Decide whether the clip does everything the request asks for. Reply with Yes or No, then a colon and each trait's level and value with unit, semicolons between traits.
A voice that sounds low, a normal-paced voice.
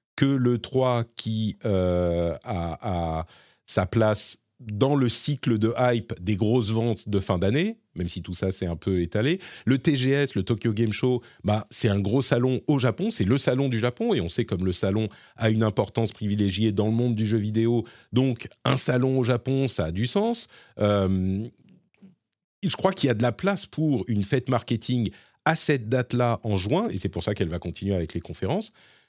Yes: low, 115 Hz; average, 205 wpm